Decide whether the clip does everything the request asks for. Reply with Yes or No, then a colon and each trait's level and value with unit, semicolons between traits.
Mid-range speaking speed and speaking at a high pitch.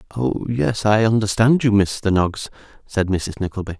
No: average, 160 wpm; low, 100 Hz